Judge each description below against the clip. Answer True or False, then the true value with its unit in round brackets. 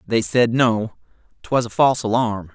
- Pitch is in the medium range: False (115 Hz)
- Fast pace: False (165 wpm)